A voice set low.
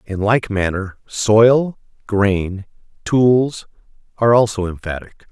Yes: low, 105 Hz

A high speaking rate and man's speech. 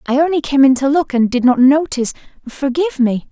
No: fast, 215 wpm; female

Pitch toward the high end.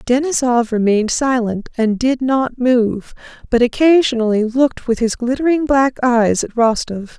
Yes: high, 245 Hz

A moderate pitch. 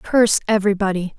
No: high, 205 Hz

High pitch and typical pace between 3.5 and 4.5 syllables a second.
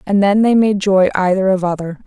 No: high, 195 Hz; 5.4 syllables/s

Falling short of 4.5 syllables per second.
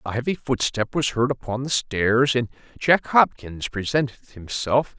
Yes: 4.3 syllables/s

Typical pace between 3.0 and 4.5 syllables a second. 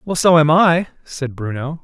Yes: 4.4 syllables/s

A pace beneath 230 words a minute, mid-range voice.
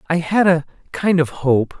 Yes: average, 200 wpm; medium, 160 Hz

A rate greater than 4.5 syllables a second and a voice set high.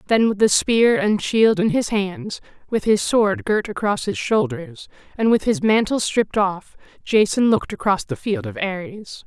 No: 4.4 syllables/s; high, 210 Hz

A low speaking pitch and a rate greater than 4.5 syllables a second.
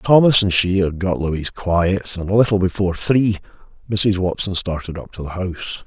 Yes: very low, 95 Hz; 5.1 syllables/s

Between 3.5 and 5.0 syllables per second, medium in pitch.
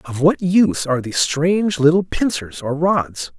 Yes: 4.9 syllables/s; medium, 160 Hz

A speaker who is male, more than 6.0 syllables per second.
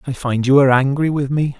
Yes: male; 6.3 syllables/s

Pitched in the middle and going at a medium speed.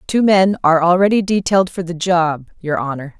Yes: medium, 175 Hz; average, 190 wpm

